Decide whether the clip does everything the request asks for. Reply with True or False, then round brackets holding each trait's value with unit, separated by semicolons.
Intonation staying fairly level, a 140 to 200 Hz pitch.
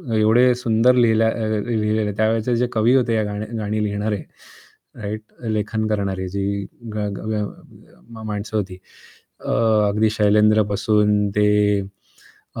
False (1.2 semitones; 110 Hz)